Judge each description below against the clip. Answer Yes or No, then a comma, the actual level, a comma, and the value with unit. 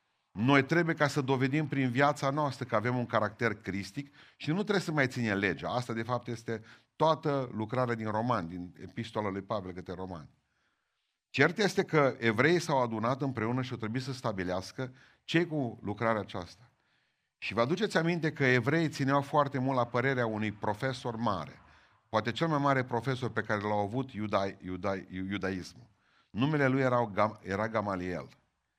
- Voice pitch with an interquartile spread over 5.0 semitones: No, average, 4.6 semitones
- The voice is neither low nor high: No, low, 120 Hz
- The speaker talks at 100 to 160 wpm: No, fast, 170 wpm